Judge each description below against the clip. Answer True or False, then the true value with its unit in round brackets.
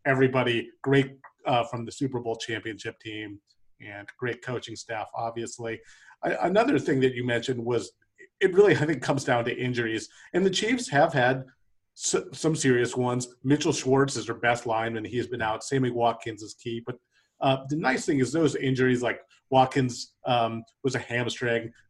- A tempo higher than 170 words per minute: True (180 wpm)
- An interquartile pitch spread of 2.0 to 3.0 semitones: True (2.6 semitones)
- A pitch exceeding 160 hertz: False (125 Hz)